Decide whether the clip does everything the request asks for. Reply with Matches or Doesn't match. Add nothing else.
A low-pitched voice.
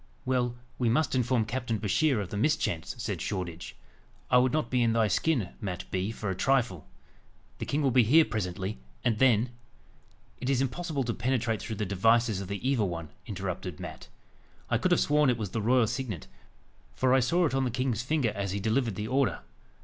Matches